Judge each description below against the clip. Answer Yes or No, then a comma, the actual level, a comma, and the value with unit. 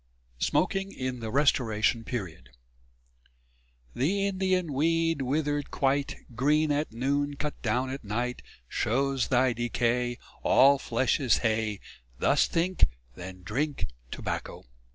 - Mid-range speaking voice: No, low, 130 Hz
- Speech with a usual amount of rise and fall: Yes, average, 4.0 semitones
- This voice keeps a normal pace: No, slow, 120 wpm